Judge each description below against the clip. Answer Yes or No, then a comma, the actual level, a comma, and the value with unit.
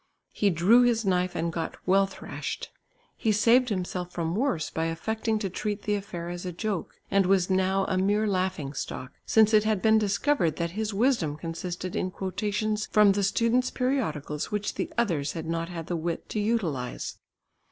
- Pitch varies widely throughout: No, average, 4.1 semitones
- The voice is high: Yes, high, 195 Hz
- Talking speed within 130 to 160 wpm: No, average, 185 wpm